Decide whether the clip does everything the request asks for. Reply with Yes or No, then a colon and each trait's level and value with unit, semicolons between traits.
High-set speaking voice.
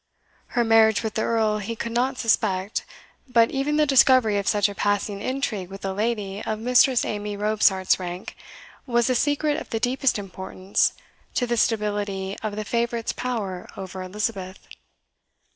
Yes: high, 215 Hz